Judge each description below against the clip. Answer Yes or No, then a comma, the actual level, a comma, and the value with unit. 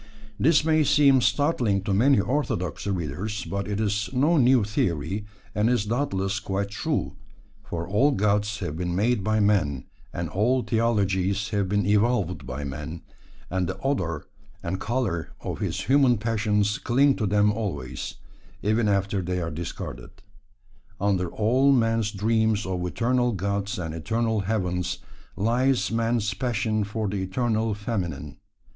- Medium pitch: No, low, 105 Hz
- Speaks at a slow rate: No, average, 150 wpm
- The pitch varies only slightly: No, average, 3.7 semitones